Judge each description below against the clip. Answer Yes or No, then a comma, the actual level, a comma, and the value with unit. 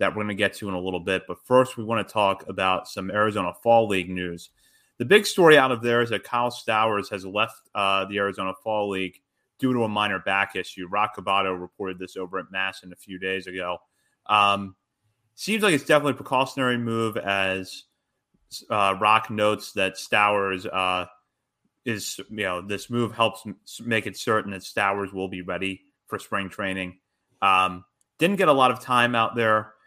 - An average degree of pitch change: Yes, average, 3.2 semitones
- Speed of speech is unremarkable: Yes, average, 195 wpm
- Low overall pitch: Yes, low, 100 Hz